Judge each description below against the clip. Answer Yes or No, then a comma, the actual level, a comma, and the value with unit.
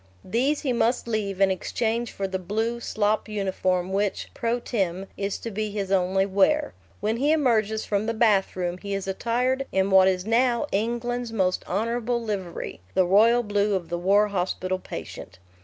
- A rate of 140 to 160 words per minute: No, average, 175 wpm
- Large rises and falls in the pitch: No, average, 3.5 semitones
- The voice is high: Yes, high, 210 Hz